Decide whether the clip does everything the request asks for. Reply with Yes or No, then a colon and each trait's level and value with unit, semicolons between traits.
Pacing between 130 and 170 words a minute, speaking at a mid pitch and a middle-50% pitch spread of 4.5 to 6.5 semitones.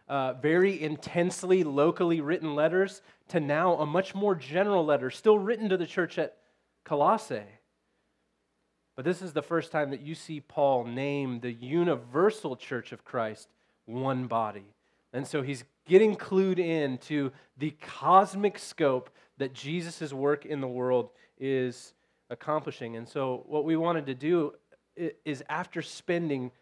Yes: average, 150 wpm; medium, 150 Hz; average, 4.8 semitones